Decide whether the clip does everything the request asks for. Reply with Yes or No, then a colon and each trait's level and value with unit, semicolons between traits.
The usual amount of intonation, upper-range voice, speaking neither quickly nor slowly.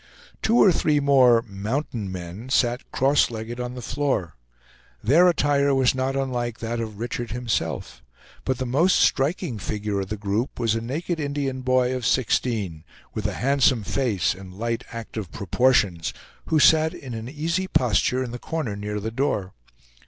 No: average, 4.2 semitones; low, 125 Hz; average, 165 wpm